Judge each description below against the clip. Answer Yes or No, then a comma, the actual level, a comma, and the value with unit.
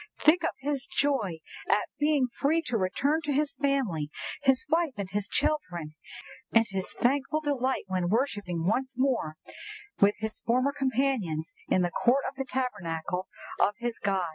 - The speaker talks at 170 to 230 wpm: No, average, 155 wpm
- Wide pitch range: Yes, wide, 6.8 semitones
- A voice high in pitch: Yes, very high, 250 Hz